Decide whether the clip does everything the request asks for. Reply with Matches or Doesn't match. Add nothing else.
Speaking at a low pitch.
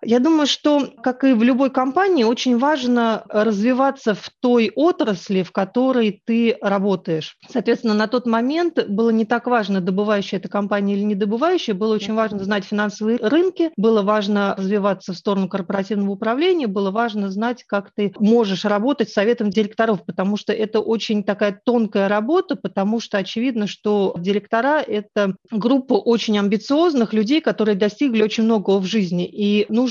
Doesn't match